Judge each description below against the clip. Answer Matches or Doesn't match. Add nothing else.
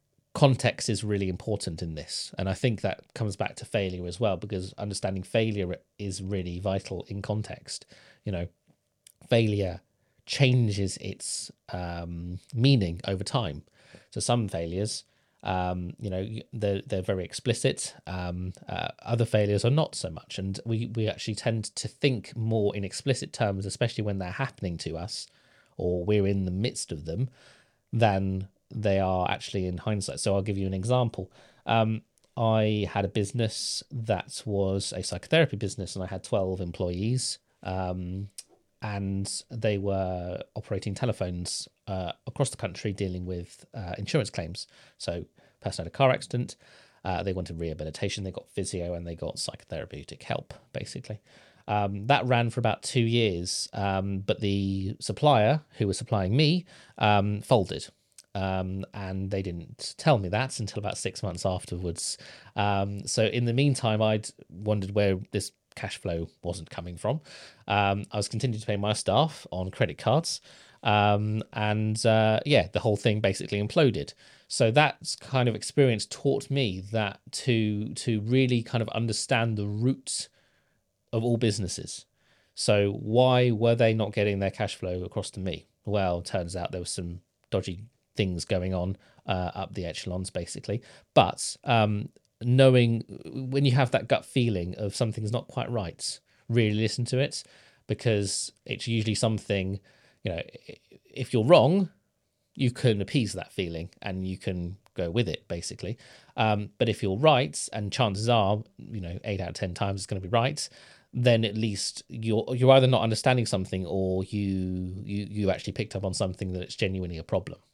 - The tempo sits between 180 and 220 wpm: Doesn't match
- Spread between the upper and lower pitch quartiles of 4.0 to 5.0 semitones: Doesn't match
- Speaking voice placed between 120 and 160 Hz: Doesn't match